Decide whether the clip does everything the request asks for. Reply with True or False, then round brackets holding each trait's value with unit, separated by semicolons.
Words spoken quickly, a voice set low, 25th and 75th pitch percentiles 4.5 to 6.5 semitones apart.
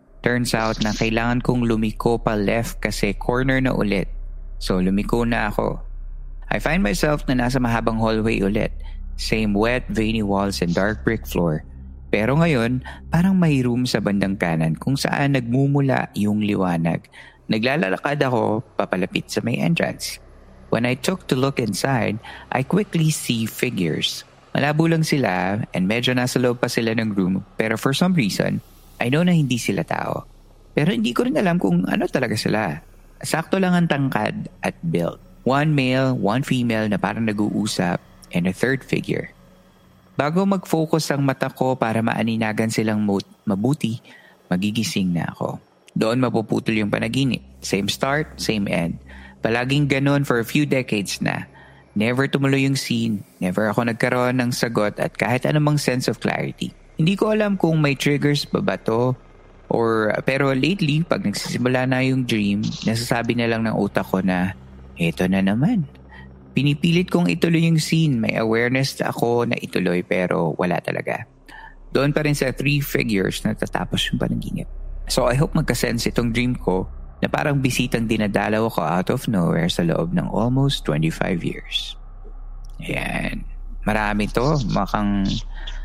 True (160 wpm; 120 Hz; 5.4 semitones)